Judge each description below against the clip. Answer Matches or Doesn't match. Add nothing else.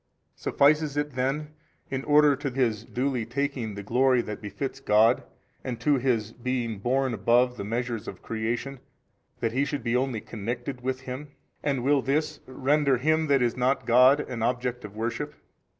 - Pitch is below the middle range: Matches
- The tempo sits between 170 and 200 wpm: Matches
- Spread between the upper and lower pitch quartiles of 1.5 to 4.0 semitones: Matches